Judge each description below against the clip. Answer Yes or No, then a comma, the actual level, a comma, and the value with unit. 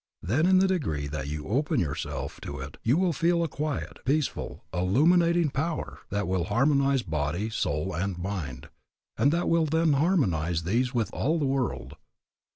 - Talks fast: No, average, 165 wpm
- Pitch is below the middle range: Yes, low, 130 Hz